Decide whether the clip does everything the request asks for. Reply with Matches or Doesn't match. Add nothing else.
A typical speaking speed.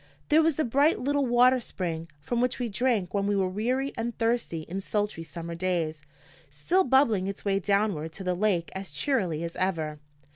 Matches